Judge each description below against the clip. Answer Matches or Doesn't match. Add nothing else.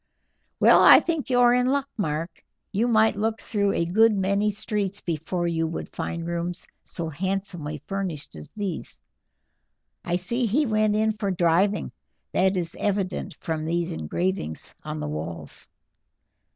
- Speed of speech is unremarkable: Matches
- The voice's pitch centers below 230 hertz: Matches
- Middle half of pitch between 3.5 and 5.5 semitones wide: Matches